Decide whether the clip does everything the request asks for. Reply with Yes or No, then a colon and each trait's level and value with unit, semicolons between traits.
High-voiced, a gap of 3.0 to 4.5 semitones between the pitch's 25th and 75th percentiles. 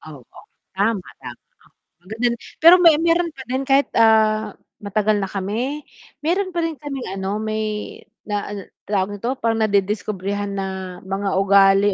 No: high, 215 Hz; average, 4.9 semitones